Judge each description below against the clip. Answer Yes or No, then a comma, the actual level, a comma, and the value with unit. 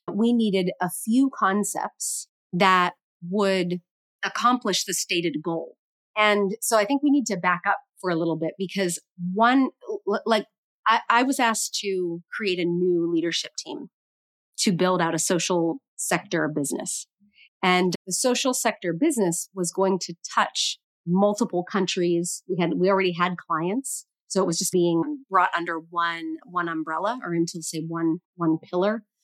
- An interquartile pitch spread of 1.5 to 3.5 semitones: Yes, average, 3.2 semitones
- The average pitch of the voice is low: No, medium, 185 Hz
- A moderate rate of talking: Yes, average, 160 wpm